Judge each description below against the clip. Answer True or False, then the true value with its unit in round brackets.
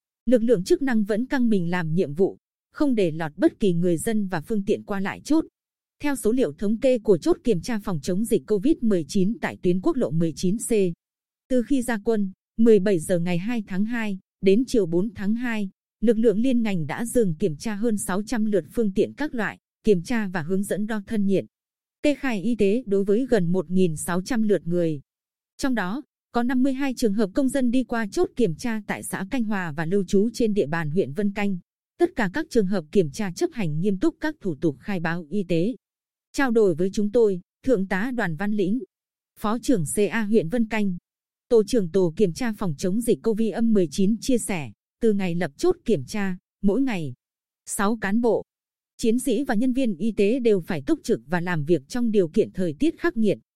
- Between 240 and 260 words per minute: False (215 wpm)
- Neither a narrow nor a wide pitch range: True (4.0 semitones)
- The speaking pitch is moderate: False (210 Hz)